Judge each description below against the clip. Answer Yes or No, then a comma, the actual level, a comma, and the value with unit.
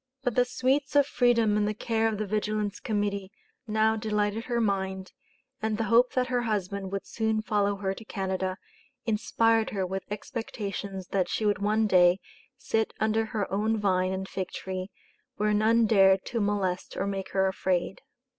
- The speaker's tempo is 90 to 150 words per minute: No, average, 175 wpm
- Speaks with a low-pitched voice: No, high, 210 Hz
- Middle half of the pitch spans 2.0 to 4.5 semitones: Yes, narrow, 2.5 semitones